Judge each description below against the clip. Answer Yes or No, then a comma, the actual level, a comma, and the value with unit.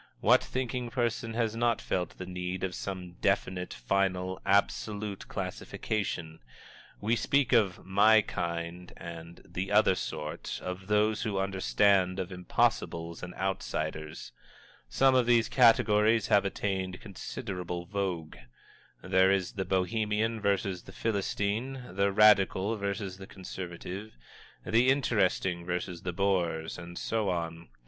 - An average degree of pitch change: Yes, average, 3.1 semitones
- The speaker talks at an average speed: No, slow, 125 wpm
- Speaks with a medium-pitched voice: No, very low, 95 Hz